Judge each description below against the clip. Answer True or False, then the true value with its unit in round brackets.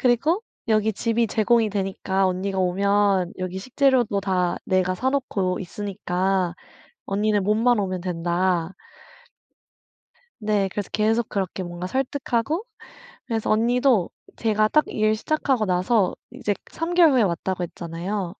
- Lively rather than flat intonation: False (4.0 semitones)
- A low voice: False (205 Hz)